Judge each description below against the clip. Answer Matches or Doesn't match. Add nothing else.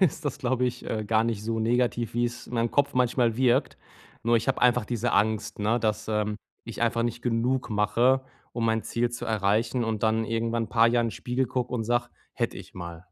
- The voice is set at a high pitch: Doesn't match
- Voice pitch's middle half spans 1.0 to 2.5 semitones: Matches